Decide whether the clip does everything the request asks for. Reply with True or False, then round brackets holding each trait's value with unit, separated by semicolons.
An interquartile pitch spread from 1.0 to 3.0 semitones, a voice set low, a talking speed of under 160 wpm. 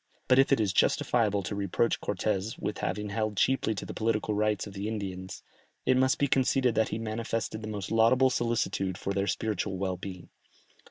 False (2.7 semitones; 110 Hz; 185 wpm)